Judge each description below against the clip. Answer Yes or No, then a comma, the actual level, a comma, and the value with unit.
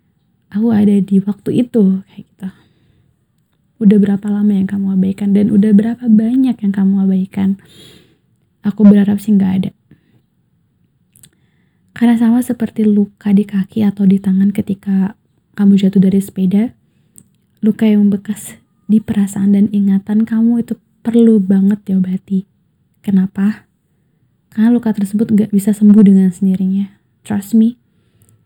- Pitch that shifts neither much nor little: No, narrow, 1.8 semitones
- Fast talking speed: No, average, 130 wpm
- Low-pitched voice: No, high, 200 Hz